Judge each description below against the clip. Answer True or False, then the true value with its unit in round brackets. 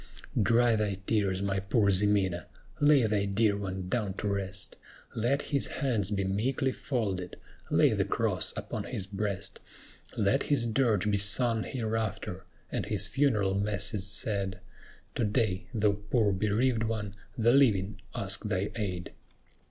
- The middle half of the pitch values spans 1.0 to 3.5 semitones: True (2.7 semitones)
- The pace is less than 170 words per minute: True (145 wpm)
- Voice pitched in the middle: False (105 Hz)